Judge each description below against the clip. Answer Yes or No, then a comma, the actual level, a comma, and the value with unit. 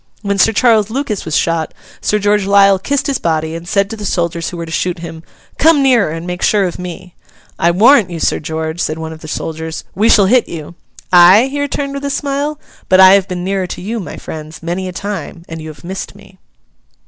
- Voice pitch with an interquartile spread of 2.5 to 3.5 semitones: No, average, 4.2 semitones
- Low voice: No, medium, 185 Hz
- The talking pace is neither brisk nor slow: No, fast, 230 wpm